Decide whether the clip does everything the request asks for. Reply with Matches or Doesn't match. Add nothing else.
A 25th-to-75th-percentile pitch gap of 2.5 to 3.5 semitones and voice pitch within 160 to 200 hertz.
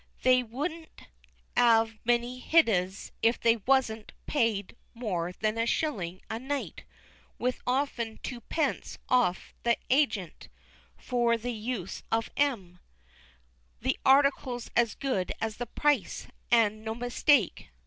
Doesn't match